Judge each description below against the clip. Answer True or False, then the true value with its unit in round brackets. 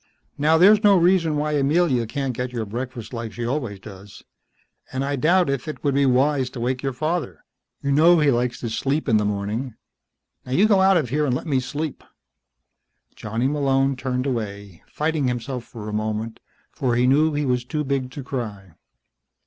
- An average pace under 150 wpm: False (195 wpm)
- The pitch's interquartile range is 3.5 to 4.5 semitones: True (4.1 semitones)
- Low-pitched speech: True (130 Hz)